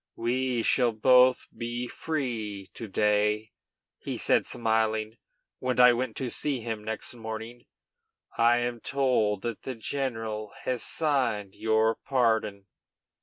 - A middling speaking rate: No, slow, 130 wpm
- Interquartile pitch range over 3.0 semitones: No, narrow, 2.4 semitones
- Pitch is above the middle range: No, low, 115 Hz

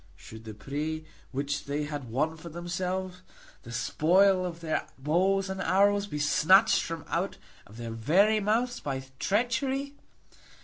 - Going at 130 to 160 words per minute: Yes, average, 145 wpm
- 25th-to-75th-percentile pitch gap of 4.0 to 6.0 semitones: Yes, wide, 5.4 semitones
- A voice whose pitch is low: No, medium, 170 Hz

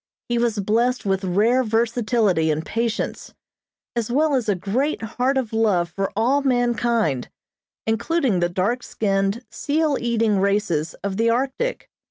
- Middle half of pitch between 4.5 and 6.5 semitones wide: No, average, 4.0 semitones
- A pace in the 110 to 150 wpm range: Yes, average, 145 wpm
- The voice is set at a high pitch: Yes, high, 225 Hz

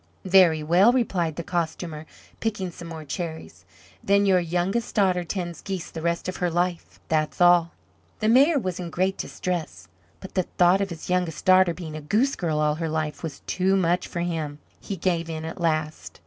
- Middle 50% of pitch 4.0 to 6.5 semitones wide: No, average, 2.7 semitones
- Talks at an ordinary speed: Yes, average, 190 wpm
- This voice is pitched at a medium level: Yes, medium, 175 Hz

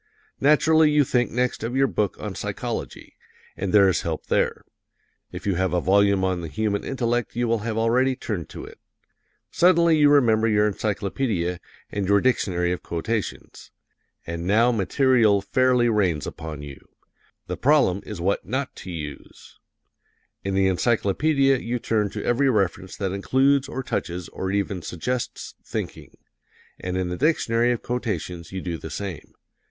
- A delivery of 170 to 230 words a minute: No, average, 160 wpm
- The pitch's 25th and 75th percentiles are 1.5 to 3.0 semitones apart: No, average, 5.2 semitones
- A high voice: No, low, 105 Hz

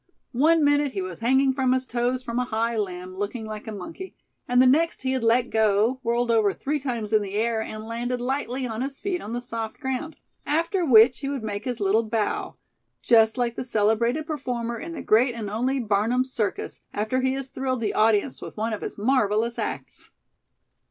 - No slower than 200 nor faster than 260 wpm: Yes, fast, 205 wpm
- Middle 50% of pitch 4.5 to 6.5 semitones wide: No, average, 3.1 semitones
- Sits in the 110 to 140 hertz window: No, high, 240 Hz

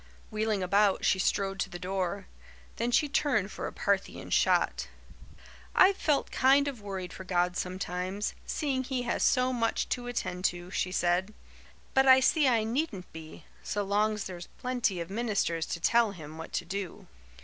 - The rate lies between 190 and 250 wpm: No, average, 170 wpm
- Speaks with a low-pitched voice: No, high, 200 Hz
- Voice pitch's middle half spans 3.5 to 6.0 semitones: Yes, average, 5.1 semitones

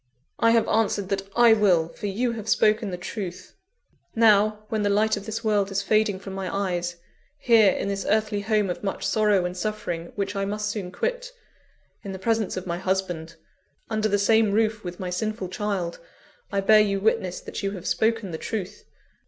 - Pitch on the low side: No, high, 205 Hz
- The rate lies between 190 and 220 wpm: Yes, average, 195 wpm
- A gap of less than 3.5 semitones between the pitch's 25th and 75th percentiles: Yes, narrow, 2.4 semitones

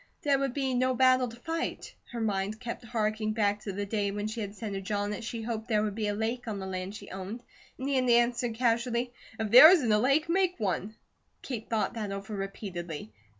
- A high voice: Yes, high, 220 Hz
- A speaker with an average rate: No, fast, 230 wpm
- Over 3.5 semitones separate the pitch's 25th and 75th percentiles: No, average, 3.2 semitones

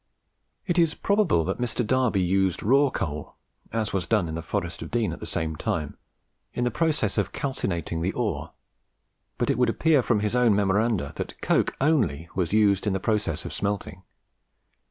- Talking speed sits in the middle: Yes, average, 185 wpm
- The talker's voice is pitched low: Yes, low, 105 Hz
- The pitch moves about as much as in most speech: No, wide, 6.0 semitones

